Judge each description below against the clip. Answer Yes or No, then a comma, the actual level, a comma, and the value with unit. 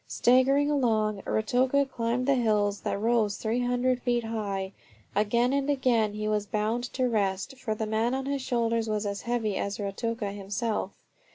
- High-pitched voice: Yes, high, 230 Hz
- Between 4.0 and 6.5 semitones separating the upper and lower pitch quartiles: No, average, 3.0 semitones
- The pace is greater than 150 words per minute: Yes, average, 165 wpm